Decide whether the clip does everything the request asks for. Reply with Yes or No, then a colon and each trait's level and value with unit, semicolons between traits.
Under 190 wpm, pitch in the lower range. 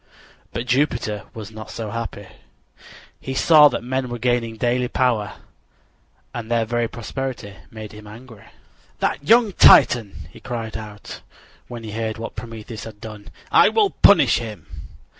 Yes: average, 155 wpm; low, 115 Hz